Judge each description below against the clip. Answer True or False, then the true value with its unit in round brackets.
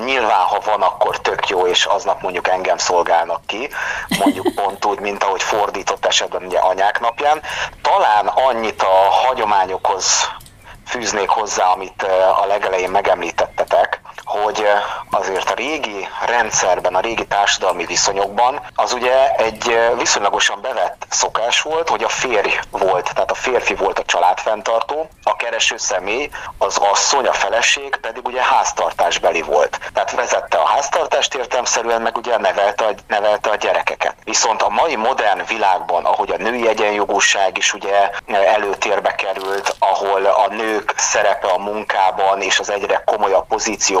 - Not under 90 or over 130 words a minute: False (145 wpm)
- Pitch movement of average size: True (3.1 semitones)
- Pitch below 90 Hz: False (105 Hz)